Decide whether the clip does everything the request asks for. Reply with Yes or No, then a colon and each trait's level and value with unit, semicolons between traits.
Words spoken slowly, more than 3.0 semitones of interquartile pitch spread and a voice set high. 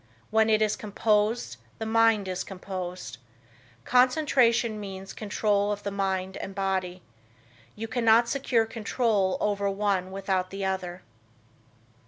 No: slow, 125 wpm; average, 2.7 semitones; high, 205 Hz